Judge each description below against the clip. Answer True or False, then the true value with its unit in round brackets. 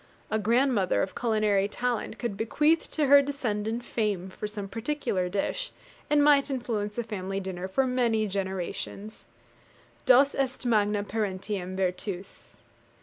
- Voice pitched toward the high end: True (215 Hz)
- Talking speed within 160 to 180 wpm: False (135 wpm)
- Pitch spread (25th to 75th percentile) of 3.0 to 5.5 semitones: True (4.2 semitones)